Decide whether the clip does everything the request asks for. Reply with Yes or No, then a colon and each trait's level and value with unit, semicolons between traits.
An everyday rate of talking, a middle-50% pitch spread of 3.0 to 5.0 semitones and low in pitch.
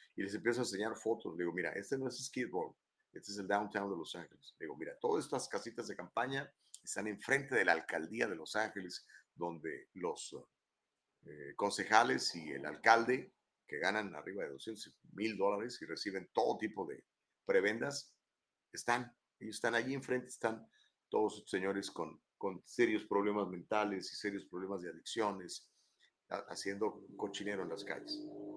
Yes: average, 170 wpm; average, 3.5 semitones; low, 105 Hz